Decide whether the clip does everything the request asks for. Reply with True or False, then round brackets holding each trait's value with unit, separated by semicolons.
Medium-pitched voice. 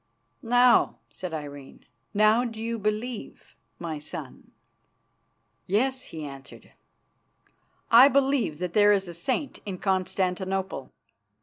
False (200 Hz)